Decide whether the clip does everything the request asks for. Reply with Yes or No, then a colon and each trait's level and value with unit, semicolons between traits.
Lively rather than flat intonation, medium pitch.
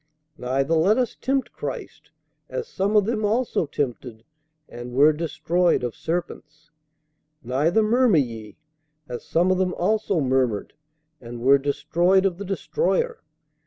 Yes: wide, 7.6 semitones; medium, 165 Hz